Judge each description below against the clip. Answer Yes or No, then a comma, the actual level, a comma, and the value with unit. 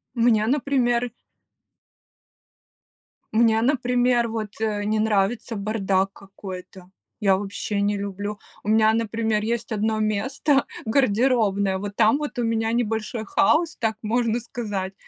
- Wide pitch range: No, average, 2.7 semitones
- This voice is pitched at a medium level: No, high, 220 Hz